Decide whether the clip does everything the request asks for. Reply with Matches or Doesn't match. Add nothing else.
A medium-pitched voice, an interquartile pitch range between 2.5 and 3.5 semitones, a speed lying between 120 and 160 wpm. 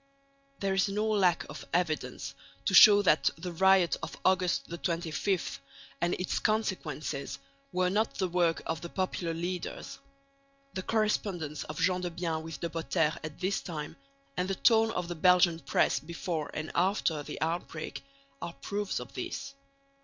Matches